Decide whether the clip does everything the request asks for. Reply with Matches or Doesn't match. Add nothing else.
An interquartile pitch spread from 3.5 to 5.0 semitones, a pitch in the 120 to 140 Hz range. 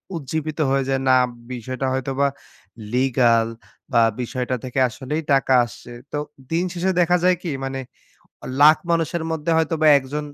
Matches